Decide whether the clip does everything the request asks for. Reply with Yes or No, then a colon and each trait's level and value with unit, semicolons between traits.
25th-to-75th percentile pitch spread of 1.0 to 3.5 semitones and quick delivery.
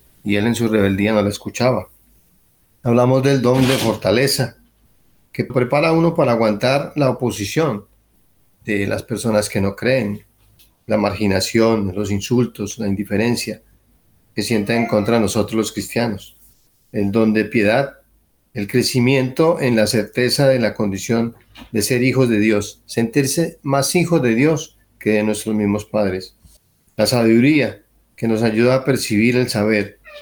No: average, 3.1 semitones; average, 150 wpm